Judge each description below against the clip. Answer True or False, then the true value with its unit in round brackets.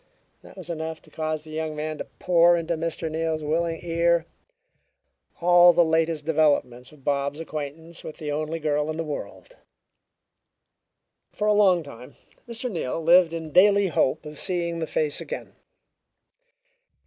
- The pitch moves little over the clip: True (1.9 semitones)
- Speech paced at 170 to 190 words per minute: False (155 wpm)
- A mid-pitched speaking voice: True (160 Hz)